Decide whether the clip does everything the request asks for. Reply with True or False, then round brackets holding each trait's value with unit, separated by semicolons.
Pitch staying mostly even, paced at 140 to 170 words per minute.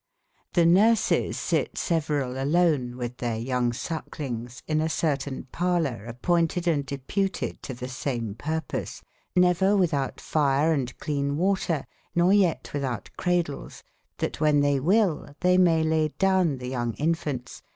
False (4.9 semitones; 150 wpm)